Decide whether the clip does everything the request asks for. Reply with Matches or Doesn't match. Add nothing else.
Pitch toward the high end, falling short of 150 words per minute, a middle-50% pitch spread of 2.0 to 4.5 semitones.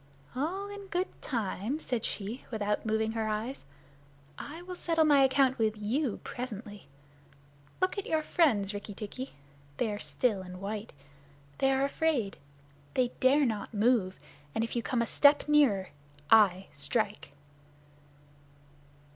Doesn't match